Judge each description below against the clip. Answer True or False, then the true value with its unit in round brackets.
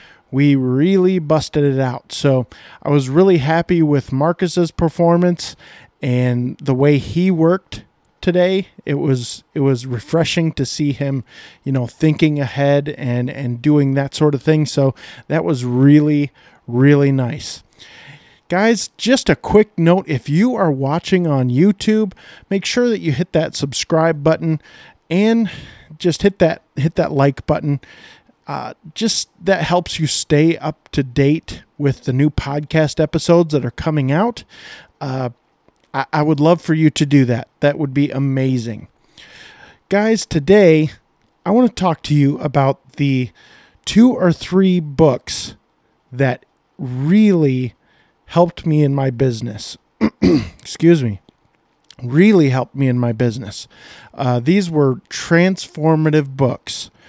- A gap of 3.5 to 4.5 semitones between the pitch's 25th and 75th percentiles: True (4.2 semitones)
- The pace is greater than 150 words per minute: False (145 wpm)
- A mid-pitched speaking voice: True (150 Hz)